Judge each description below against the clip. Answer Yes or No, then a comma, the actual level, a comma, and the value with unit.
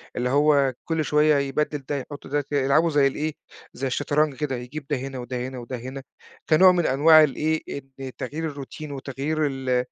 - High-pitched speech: No, medium, 140 Hz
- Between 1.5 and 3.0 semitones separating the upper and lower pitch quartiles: Yes, narrow, 2.5 semitones